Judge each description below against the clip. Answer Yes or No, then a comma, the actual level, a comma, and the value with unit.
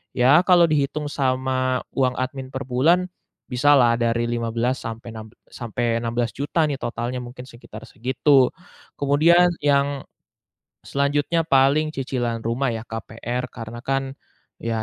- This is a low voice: Yes, low, 130 Hz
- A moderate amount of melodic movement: Yes, average, 3.2 semitones